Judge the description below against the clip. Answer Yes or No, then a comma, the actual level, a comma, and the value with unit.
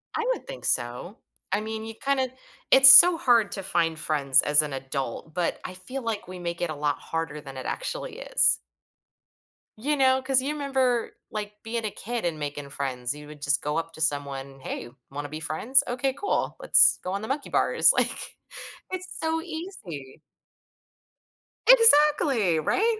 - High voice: Yes, high, 195 Hz